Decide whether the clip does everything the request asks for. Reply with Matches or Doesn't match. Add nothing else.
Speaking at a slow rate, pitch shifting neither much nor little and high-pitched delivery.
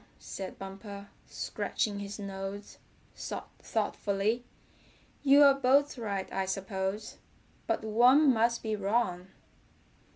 Matches